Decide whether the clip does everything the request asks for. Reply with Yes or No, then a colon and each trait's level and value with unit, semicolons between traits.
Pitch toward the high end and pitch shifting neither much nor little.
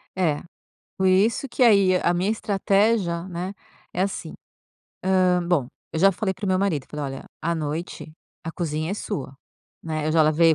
No: medium, 175 Hz; average, 3.5 semitones